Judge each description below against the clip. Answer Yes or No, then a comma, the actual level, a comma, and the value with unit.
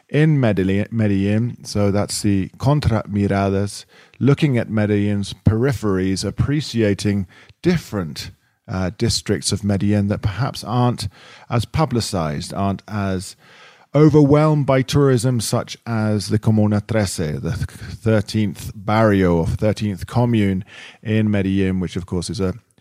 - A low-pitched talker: Yes, low, 105 Hz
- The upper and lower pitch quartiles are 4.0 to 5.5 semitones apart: No, average, 3.3 semitones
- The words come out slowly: Yes, slow, 120 wpm